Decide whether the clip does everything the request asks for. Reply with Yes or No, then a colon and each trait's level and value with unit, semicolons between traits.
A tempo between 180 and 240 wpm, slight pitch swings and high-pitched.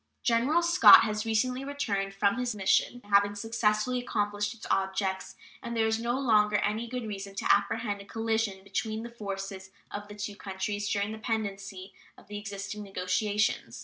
No: average, 170 wpm; narrow, 2.2 semitones; high, 210 Hz